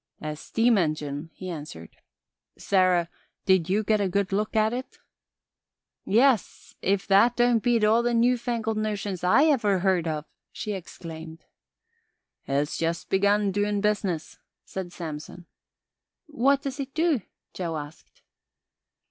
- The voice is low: No, high, 200 Hz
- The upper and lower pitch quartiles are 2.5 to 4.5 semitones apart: No, average, 5.2 semitones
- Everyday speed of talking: No, slow, 130 wpm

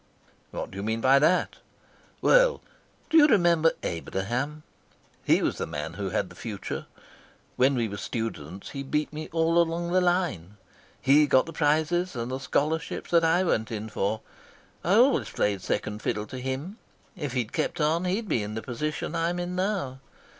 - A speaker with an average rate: Yes, average, 180 wpm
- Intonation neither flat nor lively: No, wide, 7.5 semitones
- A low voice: No, medium, 145 Hz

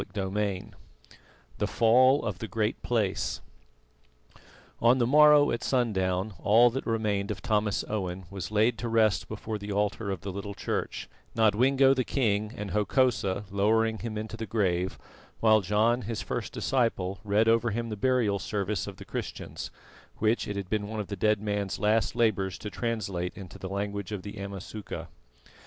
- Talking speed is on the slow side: No, average, 170 wpm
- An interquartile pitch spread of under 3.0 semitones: Yes, narrow, 2.4 semitones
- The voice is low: Yes, low, 105 Hz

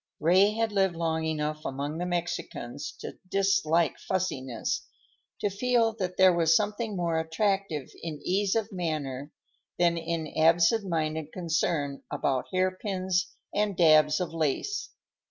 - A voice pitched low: No, medium, 170 Hz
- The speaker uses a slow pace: Yes, slow, 130 wpm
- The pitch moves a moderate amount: Yes, average, 3.8 semitones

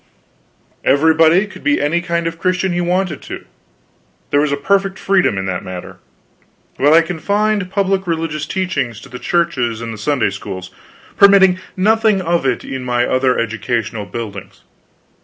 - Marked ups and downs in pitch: Yes, wide, 7.5 semitones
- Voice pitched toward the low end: No, medium, 160 Hz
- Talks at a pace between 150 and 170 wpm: Yes, average, 160 wpm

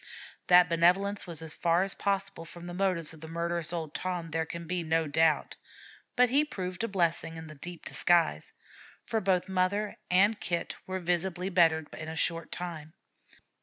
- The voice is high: No, medium, 175 Hz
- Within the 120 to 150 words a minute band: No, average, 175 wpm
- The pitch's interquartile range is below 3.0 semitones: Yes, narrow, 2.5 semitones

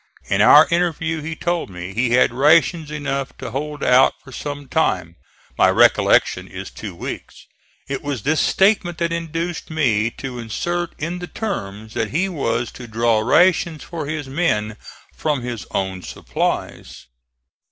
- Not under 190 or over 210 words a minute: No, average, 155 wpm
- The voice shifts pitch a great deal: Yes, wide, 5.9 semitones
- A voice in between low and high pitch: Yes, medium, 145 Hz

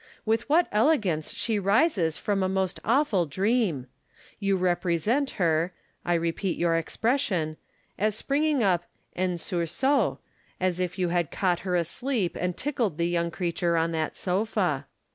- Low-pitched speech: No, medium, 185 Hz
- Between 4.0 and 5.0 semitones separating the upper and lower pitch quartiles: Yes, average, 4.7 semitones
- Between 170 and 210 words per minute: No, average, 145 wpm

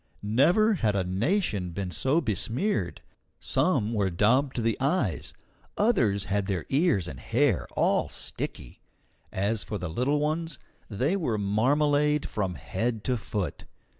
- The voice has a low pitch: Yes, low, 115 Hz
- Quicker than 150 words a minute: No, average, 140 wpm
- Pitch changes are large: Yes, wide, 7.0 semitones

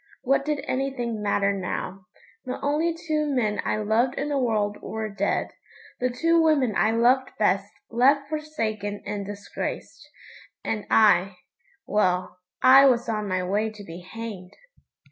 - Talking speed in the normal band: Yes, average, 145 wpm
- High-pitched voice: Yes, high, 225 Hz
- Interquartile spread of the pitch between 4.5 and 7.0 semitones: Yes, average, 5.1 semitones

